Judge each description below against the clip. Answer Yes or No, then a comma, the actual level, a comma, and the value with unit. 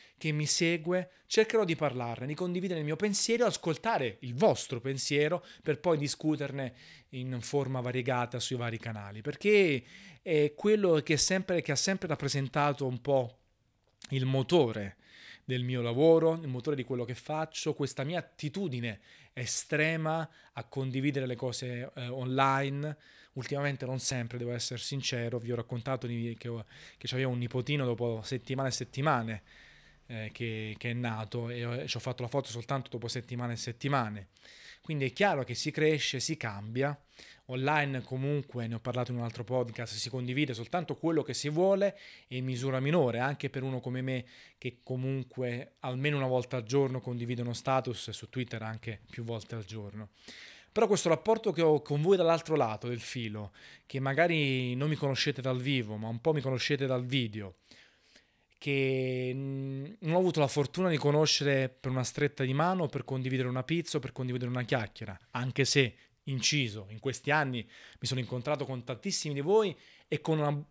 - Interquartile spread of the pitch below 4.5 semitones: Yes, average, 3.5 semitones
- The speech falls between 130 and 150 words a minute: No, fast, 170 wpm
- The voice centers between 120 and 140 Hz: Yes, low, 130 Hz